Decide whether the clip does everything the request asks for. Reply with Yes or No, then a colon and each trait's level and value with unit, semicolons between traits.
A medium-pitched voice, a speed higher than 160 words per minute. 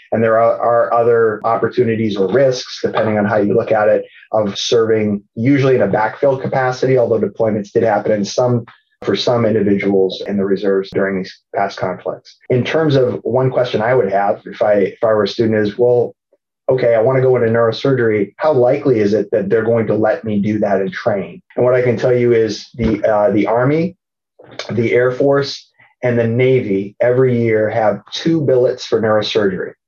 No: low, 115 Hz; average, 200 wpm